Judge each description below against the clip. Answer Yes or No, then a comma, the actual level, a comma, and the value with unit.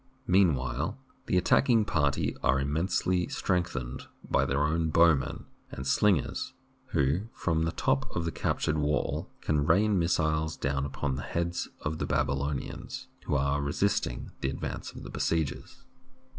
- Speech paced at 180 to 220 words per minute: No, average, 155 wpm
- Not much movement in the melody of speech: No, average, 3.7 semitones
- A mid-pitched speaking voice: No, very low, 75 Hz